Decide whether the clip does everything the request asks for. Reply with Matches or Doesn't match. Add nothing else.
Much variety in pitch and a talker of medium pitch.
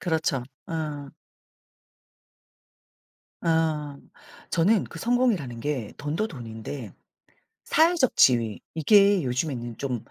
Matches